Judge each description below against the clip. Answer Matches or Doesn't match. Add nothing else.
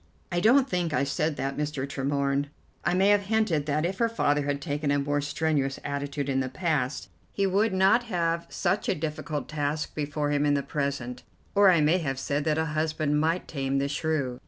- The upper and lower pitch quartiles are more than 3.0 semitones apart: Matches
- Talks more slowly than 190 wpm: Doesn't match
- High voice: Doesn't match